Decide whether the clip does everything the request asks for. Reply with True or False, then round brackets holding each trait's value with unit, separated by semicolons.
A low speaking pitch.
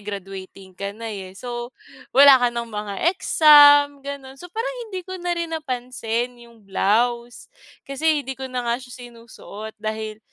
False (245 Hz)